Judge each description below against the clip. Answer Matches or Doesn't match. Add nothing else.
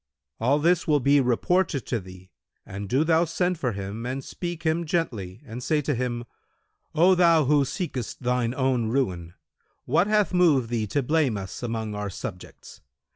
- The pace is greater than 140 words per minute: Matches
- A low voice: Matches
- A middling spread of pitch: Doesn't match